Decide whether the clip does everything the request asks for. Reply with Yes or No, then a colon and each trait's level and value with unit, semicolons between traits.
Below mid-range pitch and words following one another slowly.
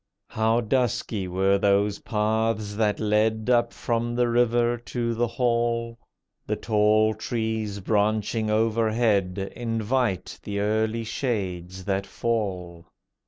Yes: low, 110 Hz; slow, 115 wpm